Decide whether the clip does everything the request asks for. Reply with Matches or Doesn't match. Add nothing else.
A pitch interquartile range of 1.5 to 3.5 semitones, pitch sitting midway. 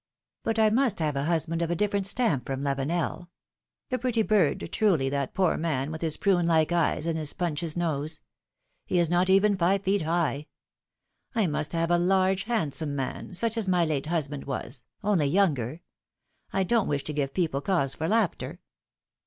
Doesn't match